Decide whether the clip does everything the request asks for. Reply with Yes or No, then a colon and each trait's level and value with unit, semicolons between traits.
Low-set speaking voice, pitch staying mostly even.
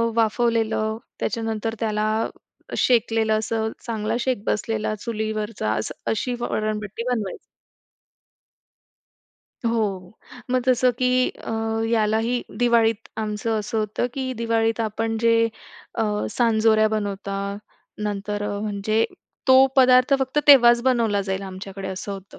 No: high, 220 Hz; narrow, 1.9 semitones